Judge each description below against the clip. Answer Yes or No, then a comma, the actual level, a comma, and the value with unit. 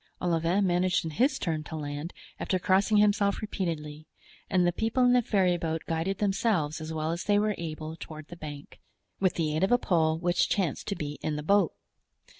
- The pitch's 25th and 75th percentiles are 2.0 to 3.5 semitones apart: No, average, 4.1 semitones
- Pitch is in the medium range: Yes, medium, 175 Hz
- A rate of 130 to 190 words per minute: No, average, 200 wpm